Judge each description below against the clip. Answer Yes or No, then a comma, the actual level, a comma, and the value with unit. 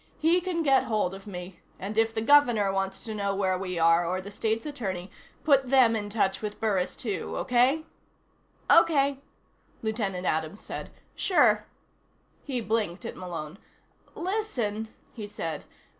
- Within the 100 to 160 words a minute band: Yes, average, 150 wpm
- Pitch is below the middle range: No, high, 215 Hz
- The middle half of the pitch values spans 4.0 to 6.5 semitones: Yes, average, 5.3 semitones